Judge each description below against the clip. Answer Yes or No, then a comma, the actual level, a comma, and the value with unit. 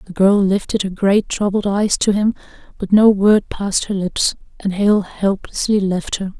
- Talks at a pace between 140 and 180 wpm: No, average, 190 wpm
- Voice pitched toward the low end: No, high, 200 Hz